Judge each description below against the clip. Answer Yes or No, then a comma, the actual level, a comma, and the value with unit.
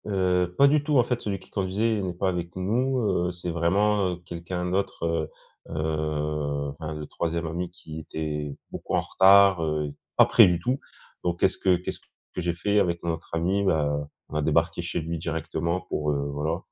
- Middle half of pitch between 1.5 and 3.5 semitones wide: Yes, average, 3.2 semitones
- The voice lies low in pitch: Yes, very low, 85 Hz